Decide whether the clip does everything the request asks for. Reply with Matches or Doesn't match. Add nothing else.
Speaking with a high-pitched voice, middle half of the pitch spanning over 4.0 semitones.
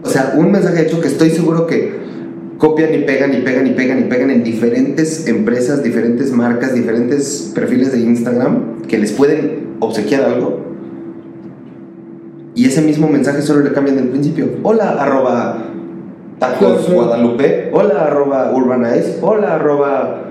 Doesn't match